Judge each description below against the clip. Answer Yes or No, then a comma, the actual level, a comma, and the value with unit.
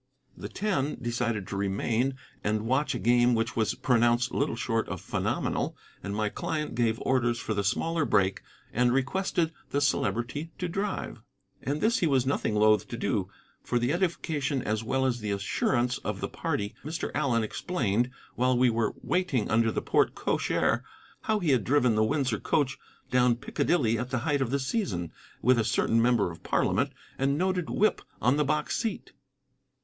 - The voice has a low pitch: Yes, low, 125 Hz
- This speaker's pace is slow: No, average, 180 wpm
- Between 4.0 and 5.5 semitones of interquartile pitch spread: Yes, average, 4.4 semitones